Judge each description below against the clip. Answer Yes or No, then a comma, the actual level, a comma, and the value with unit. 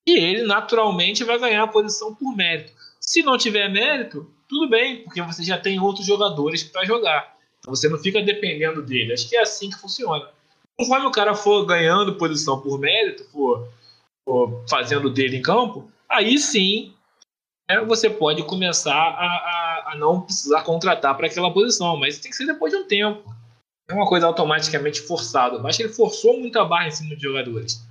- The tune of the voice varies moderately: No, wide, 6.4 semitones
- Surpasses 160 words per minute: Yes, fast, 185 wpm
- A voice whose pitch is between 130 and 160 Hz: No, medium, 175 Hz